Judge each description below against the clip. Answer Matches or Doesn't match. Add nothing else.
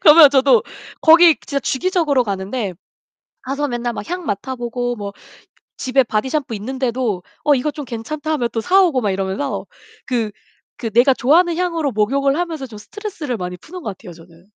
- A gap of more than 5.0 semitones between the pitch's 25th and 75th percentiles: Matches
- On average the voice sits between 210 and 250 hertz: Doesn't match